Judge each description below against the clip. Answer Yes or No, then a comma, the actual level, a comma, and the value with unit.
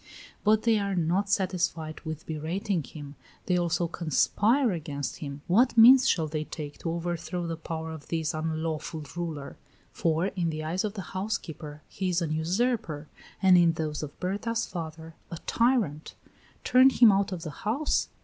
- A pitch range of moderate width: Yes, average, 4.0 semitones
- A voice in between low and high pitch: Yes, medium, 170 Hz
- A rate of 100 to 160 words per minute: No, average, 170 wpm